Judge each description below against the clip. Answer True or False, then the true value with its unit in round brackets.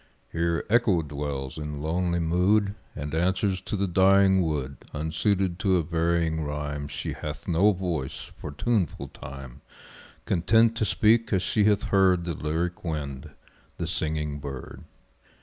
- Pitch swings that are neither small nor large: True (4.4 semitones)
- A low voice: True (85 Hz)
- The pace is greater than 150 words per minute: False (145 wpm)